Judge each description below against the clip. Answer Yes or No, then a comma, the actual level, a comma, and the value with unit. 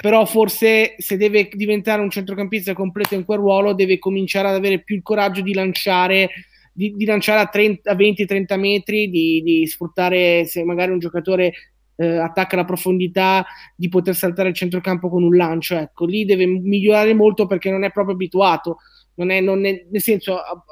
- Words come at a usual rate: No, fast, 175 wpm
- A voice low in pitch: No, high, 190 Hz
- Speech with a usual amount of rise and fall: No, narrow, 2.1 semitones